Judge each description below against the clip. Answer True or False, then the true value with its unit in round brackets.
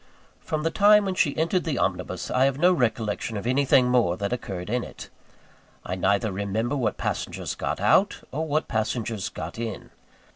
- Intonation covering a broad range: True (6.2 semitones)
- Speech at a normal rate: True (180 wpm)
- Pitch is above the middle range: False (125 Hz)